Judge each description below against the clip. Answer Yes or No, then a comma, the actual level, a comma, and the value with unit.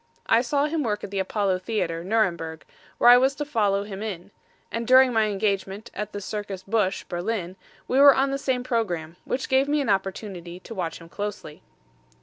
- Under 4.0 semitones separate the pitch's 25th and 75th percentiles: No, average, 4.6 semitones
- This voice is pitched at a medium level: No, high, 210 Hz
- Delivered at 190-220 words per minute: Yes, average, 195 wpm